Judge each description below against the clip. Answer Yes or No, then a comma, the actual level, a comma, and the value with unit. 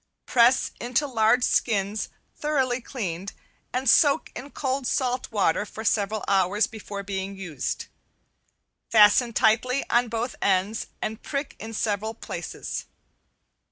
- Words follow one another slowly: Yes, slow, 125 wpm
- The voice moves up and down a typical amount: Yes, average, 3.8 semitones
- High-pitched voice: Yes, high, 225 Hz